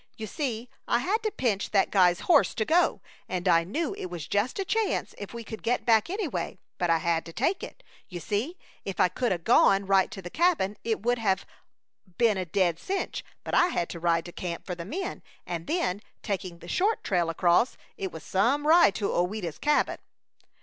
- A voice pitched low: No, high, 200 Hz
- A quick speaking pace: Yes, fast, 210 wpm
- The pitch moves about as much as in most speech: No, wide, 7.3 semitones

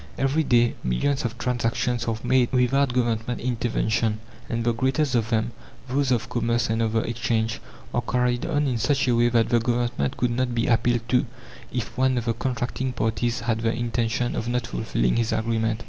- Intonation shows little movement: Yes, narrow, 1.6 semitones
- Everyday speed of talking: Yes, average, 195 wpm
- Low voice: Yes, low, 120 Hz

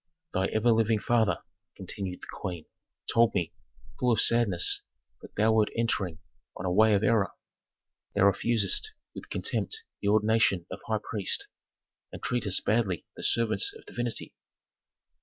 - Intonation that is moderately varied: Yes, average, 3.0 semitones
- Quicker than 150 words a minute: No, average, 145 wpm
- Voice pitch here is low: Yes, low, 110 Hz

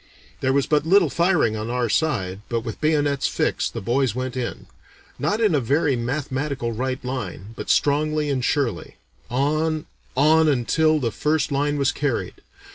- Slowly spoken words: No, average, 165 wpm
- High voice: No, medium, 140 Hz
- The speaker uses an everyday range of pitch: Yes, average, 3.8 semitones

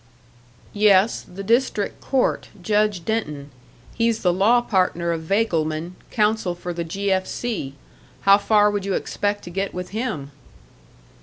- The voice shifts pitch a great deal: No, average, 3.5 semitones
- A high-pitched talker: Yes, high, 195 Hz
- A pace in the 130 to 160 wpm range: Yes, average, 145 wpm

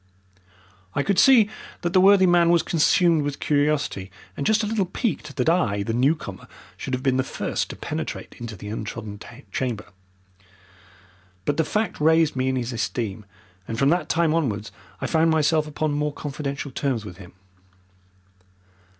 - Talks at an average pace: Yes, average, 165 wpm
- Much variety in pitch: Yes, wide, 5.9 semitones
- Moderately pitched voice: Yes, medium, 145 Hz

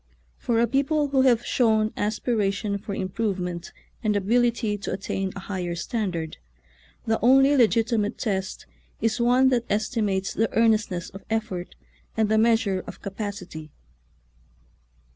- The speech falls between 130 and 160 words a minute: Yes, average, 140 wpm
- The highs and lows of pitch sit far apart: No, average, 3.3 semitones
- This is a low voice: No, high, 215 Hz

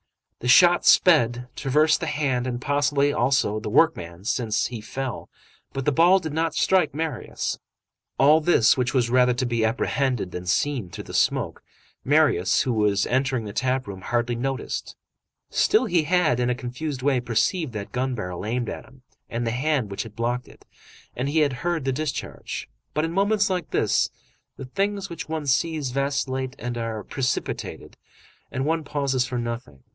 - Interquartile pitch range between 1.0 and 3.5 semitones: No, average, 4.1 semitones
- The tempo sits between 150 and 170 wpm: No, average, 180 wpm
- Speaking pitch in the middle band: No, low, 130 Hz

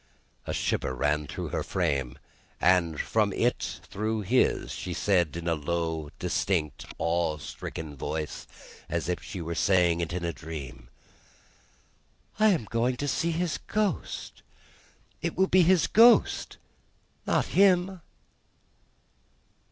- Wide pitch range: Yes, wide, 8.1 semitones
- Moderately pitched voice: No, very low, 85 Hz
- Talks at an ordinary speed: No, slow, 130 wpm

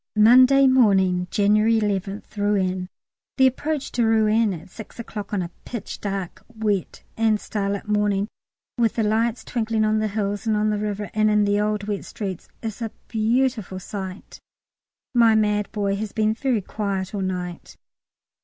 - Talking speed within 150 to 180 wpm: Yes, average, 165 wpm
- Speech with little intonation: Yes, narrow, 2.0 semitones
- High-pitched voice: Yes, high, 210 Hz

